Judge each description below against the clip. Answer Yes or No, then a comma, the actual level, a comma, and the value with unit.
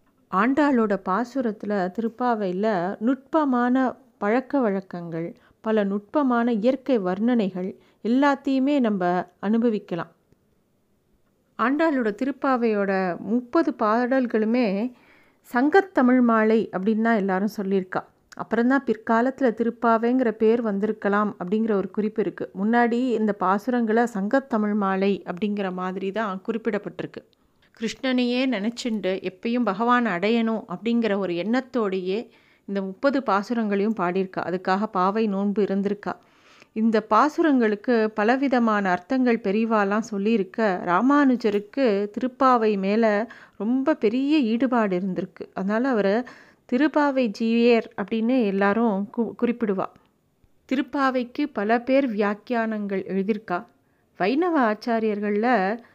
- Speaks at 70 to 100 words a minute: Yes, average, 95 wpm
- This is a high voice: Yes, high, 225 Hz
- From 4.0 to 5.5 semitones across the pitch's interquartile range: No, average, 3.6 semitones